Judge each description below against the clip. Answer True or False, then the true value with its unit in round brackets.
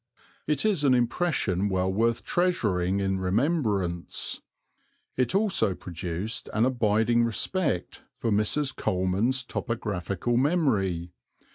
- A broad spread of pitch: True (5.8 semitones)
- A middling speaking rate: False (105 wpm)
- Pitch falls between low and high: False (110 Hz)